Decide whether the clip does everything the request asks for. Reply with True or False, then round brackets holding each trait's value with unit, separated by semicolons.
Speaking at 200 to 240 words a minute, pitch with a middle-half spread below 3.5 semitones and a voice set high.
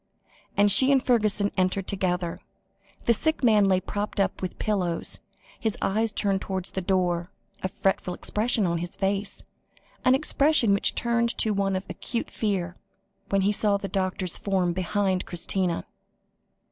False (155 wpm; 2.5 semitones; 195 Hz)